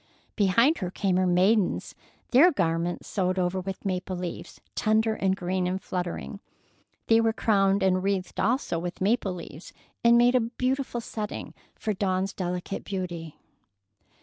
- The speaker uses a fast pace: No, average, 150 wpm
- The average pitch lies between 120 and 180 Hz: No, high, 190 Hz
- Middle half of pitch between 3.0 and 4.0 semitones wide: Yes, average, 3.5 semitones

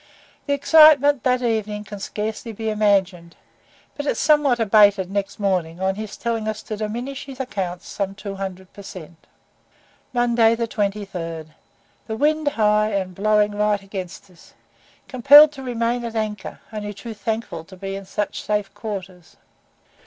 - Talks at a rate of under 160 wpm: Yes, average, 150 wpm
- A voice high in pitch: Yes, high, 210 Hz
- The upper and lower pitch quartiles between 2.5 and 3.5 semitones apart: Yes, average, 3.1 semitones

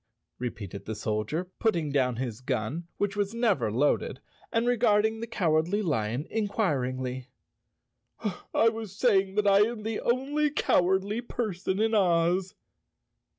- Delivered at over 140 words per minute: No, slow, 135 wpm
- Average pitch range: No, wide, 8.8 semitones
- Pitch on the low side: No, high, 190 Hz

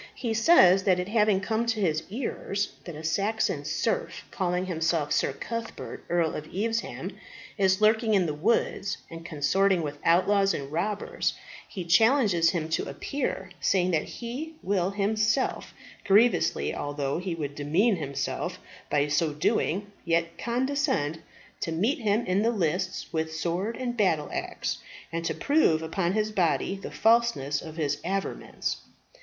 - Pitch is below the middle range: No, high, 190 Hz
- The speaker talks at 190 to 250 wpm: No, average, 150 wpm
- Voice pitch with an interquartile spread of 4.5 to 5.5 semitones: Yes, average, 5.1 semitones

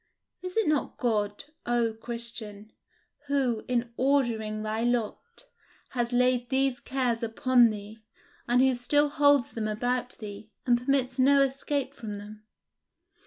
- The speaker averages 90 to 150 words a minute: Yes, slow, 135 wpm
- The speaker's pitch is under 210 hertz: No, high, 245 Hz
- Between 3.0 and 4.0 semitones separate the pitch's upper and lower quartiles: Yes, average, 3.3 semitones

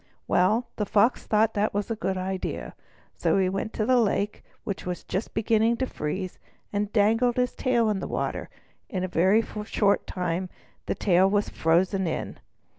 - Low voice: No, high, 205 Hz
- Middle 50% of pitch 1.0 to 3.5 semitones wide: Yes, average, 3.1 semitones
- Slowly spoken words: No, average, 175 wpm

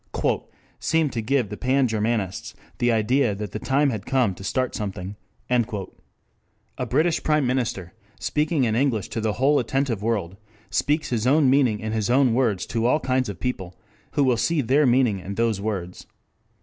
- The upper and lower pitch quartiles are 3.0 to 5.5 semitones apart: Yes, average, 4.2 semitones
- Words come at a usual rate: Yes, average, 180 wpm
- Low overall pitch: Yes, low, 120 Hz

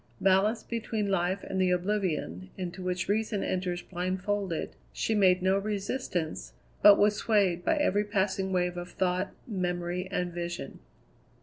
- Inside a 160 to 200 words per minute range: No, average, 140 wpm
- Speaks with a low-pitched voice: No, medium, 185 Hz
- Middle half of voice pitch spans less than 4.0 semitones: Yes, narrow, 2.4 semitones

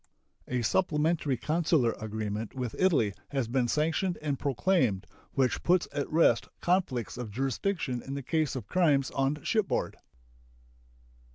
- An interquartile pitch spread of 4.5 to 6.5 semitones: Yes, average, 5.2 semitones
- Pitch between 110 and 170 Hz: Yes, medium, 140 Hz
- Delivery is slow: Yes, slow, 130 wpm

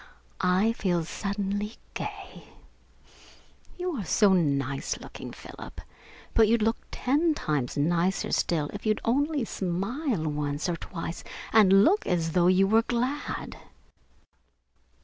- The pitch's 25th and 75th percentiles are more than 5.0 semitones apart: Yes, wide, 5.4 semitones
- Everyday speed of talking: No, slow, 125 wpm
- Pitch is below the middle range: No, high, 195 Hz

